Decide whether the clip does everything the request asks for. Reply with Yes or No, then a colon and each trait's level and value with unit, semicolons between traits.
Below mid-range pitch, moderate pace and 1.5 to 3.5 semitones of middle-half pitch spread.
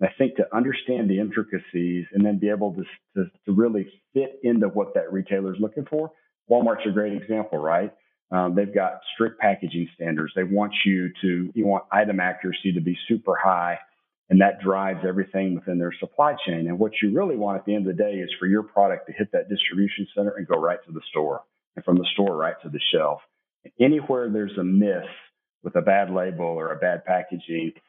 No: low, 100 Hz; fast, 215 wpm; narrow, 2.6 semitones